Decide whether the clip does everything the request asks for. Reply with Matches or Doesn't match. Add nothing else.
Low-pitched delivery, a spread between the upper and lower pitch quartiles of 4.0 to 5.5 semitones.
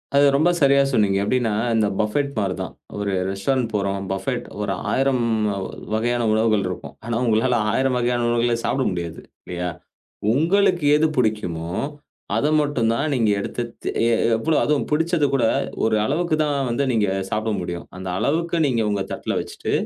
Matches